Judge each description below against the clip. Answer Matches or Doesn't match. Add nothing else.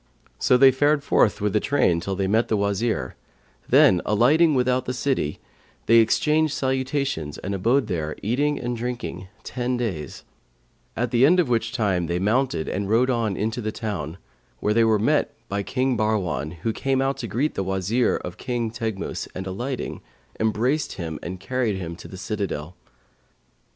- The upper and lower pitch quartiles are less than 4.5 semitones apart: Doesn't match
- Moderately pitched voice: Doesn't match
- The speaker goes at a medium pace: Matches